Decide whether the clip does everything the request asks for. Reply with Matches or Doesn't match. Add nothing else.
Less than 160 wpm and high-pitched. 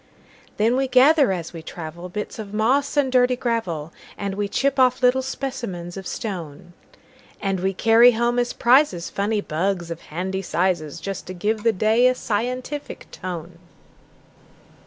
Matches